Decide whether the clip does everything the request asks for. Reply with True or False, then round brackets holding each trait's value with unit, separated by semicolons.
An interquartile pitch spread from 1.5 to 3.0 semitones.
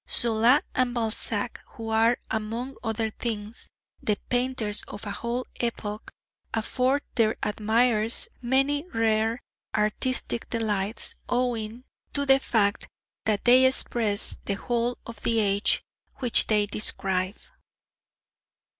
True (2.5 semitones)